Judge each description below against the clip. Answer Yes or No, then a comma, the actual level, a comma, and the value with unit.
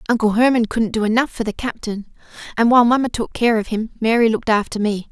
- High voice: Yes, high, 225 Hz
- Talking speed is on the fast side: Yes, fast, 225 wpm